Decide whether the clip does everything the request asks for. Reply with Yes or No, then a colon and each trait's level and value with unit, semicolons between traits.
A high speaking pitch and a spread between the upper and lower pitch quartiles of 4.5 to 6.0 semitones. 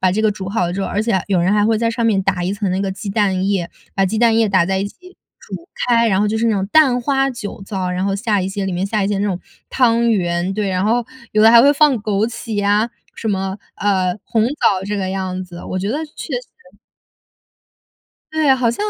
No: high, 205 Hz; average, 3.3 semitones